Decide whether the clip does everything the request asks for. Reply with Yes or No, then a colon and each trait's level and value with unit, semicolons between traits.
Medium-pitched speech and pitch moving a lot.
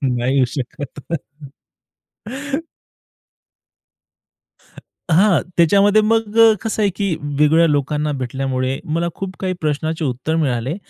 Yes: medium, 155 Hz; wide, 6.2 semitones